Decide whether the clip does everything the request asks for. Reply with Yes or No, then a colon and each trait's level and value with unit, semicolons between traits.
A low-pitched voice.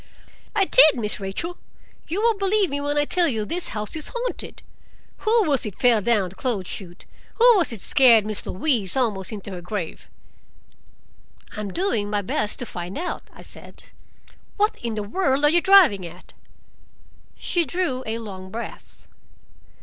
No: high, 240 Hz